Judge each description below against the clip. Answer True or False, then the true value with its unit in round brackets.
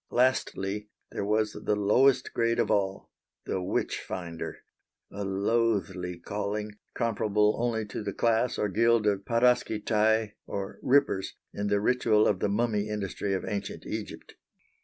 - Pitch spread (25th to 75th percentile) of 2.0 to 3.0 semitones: True (2.5 semitones)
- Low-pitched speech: True (105 Hz)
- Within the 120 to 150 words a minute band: True (140 wpm)